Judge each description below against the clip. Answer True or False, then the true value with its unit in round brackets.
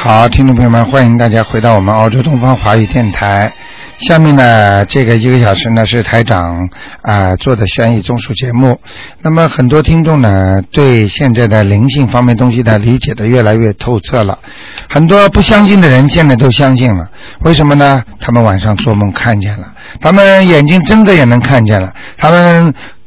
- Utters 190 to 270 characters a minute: False (290 characters per minute)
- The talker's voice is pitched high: False (120 Hz)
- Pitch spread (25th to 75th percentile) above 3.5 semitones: True (4.2 semitones)